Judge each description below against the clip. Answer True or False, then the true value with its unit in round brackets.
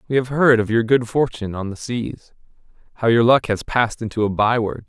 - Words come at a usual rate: False (210 wpm)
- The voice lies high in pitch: False (115 Hz)